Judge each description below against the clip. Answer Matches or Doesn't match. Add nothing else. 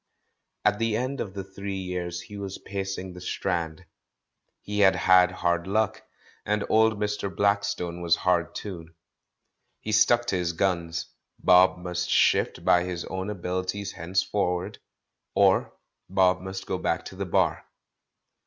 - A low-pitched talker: Matches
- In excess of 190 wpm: Doesn't match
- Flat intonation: Matches